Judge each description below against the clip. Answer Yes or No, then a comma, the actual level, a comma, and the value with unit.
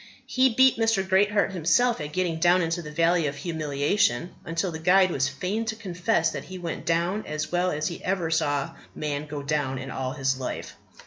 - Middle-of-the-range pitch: Yes, medium, 170 Hz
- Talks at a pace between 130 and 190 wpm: No, average, 200 wpm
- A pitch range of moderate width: Yes, average, 4.0 semitones